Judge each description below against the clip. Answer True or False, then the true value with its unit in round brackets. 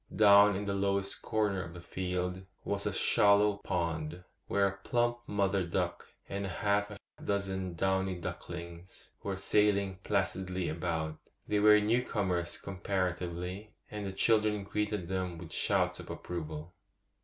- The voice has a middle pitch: False (95 Hz)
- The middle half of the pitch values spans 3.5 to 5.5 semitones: False (2.5 semitones)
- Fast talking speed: False (145 wpm)